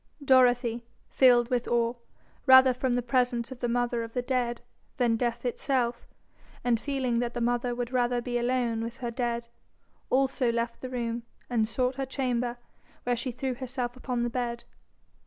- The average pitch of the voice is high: Yes, high, 245 Hz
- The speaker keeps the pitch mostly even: Yes, narrow, 1.2 semitones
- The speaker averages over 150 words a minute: Yes, average, 175 wpm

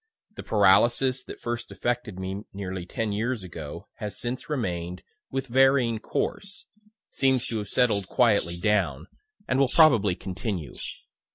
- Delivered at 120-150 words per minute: Yes, average, 140 wpm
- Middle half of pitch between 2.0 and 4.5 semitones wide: No, average, 4.9 semitones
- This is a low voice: Yes, low, 110 Hz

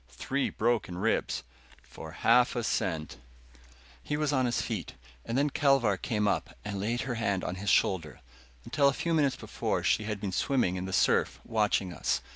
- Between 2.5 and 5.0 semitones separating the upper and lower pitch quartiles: No, wide, 5.6 semitones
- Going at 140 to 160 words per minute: No, average, 190 wpm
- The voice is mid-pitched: No, low, 105 Hz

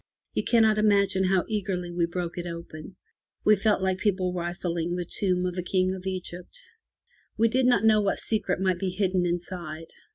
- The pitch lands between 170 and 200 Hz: Yes, medium, 185 Hz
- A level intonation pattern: Yes, narrow, 2.3 semitones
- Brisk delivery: No, average, 185 wpm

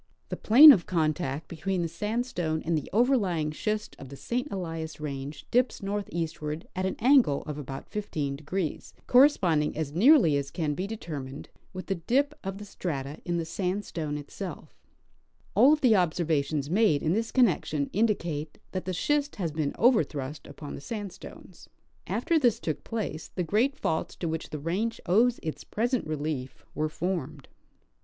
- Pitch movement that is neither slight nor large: No, wide, 5.9 semitones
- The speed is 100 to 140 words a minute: No, average, 165 wpm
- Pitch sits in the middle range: Yes, medium, 170 Hz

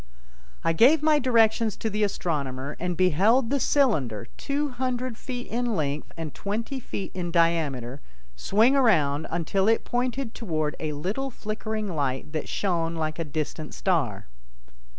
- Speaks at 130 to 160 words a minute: Yes, average, 150 wpm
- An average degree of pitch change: No, wide, 7.5 semitones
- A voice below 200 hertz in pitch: Yes, high, 190 Hz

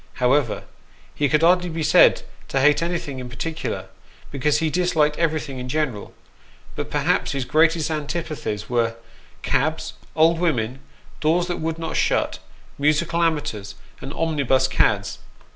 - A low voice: No, medium, 150 Hz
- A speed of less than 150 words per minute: Yes, average, 140 wpm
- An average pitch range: Yes, average, 3.7 semitones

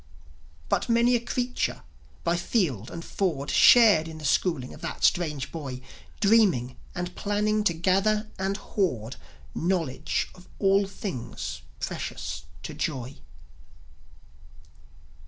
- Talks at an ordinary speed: No, slow, 120 wpm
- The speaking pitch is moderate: Yes, medium, 175 Hz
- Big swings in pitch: Yes, wide, 7.1 semitones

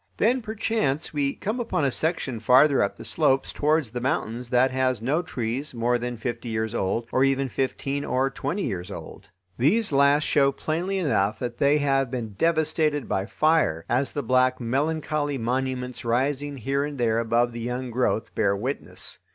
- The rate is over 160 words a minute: Yes, average, 175 wpm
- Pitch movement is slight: No, average, 3.6 semitones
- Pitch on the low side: Yes, low, 130 Hz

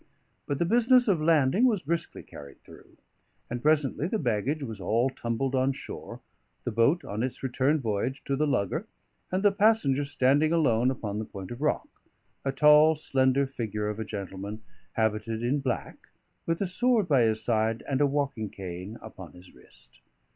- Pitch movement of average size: No, wide, 5.7 semitones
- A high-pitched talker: No, low, 130 Hz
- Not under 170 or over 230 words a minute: Yes, average, 175 wpm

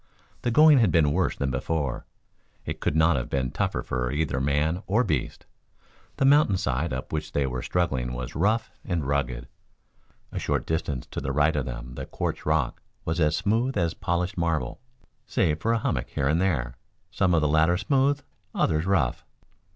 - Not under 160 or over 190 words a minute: Yes, average, 185 wpm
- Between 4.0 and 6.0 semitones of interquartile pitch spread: Yes, average, 5.2 semitones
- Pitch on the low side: Yes, very low, 80 Hz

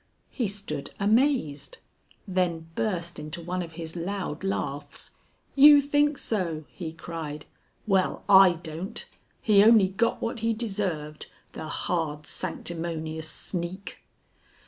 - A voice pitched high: No, medium, 180 Hz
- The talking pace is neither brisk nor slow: No, slow, 120 wpm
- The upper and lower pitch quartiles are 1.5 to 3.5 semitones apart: No, average, 4.3 semitones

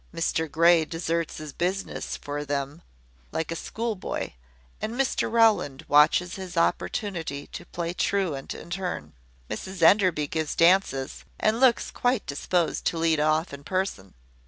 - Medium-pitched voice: Yes, medium, 170 Hz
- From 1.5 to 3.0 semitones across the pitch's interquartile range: No, average, 4.1 semitones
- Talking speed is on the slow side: No, average, 145 wpm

